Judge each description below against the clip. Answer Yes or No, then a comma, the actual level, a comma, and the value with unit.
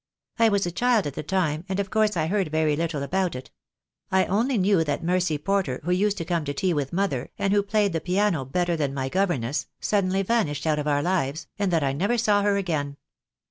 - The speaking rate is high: Yes, fast, 230 wpm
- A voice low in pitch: No, medium, 180 Hz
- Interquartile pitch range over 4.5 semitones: Yes, average, 4.9 semitones